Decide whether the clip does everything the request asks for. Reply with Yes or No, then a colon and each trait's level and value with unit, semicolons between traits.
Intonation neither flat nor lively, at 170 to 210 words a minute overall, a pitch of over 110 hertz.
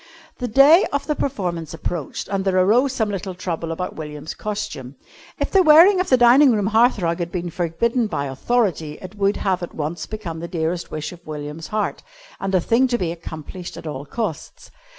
No: wide, 6.1 semitones; average, 200 wpm; medium, 185 Hz